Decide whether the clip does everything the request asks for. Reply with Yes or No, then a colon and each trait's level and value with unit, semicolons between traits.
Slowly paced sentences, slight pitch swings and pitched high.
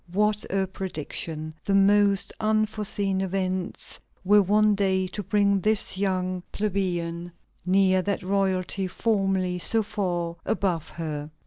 Yes: slow, 120 wpm; narrow, 2.0 semitones; high, 195 Hz